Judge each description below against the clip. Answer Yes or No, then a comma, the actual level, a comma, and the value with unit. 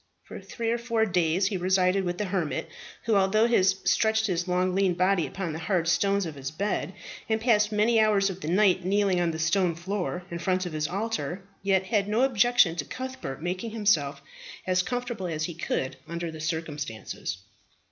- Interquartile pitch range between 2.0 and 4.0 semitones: Yes, average, 3.6 semitones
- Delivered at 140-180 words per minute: No, average, 195 wpm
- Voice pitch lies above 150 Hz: Yes, high, 190 Hz